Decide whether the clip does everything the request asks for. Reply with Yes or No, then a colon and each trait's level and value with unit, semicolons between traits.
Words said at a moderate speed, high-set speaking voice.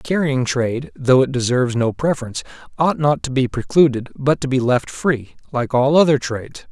No: average, 195 wpm; low, 135 Hz